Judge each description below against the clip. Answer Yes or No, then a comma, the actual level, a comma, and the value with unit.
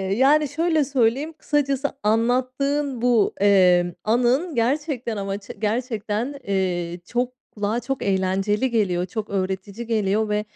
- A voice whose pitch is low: No, high, 225 Hz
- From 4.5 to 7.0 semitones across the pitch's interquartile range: Yes, average, 4.8 semitones